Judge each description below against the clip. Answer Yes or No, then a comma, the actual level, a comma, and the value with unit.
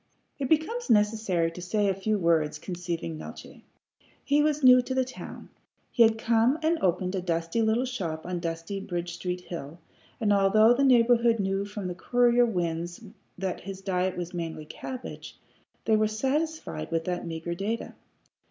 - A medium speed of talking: Yes, average, 170 wpm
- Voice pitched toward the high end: Yes, high, 195 Hz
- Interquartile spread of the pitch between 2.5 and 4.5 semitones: No, average, 5.3 semitones